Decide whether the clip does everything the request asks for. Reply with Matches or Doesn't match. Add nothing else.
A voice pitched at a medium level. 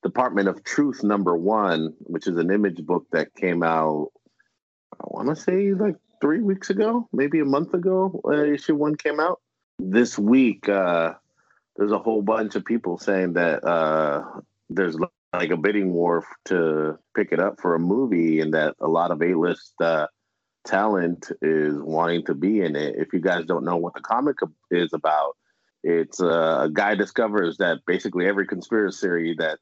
Doesn't match